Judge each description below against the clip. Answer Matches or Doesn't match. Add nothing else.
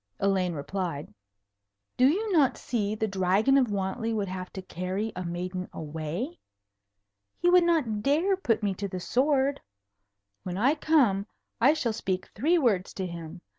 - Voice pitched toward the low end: Doesn't match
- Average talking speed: Matches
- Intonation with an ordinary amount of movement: Doesn't match